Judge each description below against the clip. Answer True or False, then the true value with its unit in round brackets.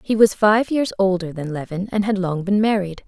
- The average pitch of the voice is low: False (195 Hz)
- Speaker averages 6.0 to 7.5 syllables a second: False (5.1 syllables/s)